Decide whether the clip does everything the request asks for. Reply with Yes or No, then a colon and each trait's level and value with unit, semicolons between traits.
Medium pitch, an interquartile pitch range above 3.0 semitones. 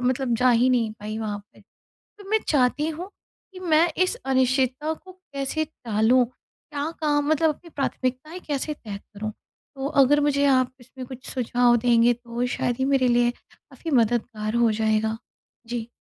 No: very high, 255 Hz; average, 3.7 semitones